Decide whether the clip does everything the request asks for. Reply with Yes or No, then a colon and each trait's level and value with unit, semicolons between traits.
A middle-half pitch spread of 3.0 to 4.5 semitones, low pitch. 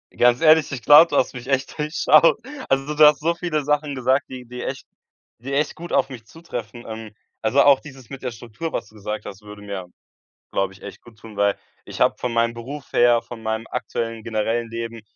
Yes: average, 4.1 semitones; low, 125 Hz